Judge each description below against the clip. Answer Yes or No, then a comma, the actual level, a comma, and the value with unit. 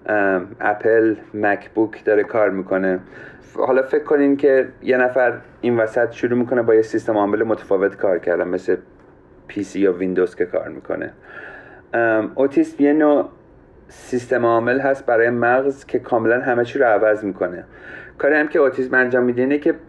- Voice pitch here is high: No, low, 120 Hz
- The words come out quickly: Yes, fast, 170 wpm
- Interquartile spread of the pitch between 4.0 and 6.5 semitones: No, average, 3.6 semitones